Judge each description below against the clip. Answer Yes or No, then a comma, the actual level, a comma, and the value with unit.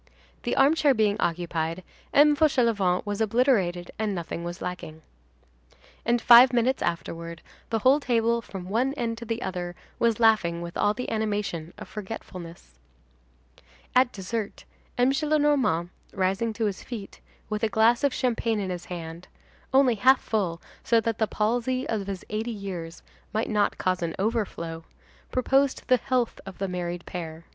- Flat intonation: No, average, 5.1 semitones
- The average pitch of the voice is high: Yes, high, 215 Hz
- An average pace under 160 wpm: Yes, average, 150 wpm